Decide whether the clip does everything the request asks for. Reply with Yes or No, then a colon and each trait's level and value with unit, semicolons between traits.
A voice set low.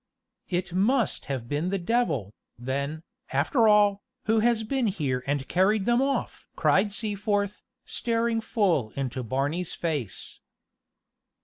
No: high, 190 Hz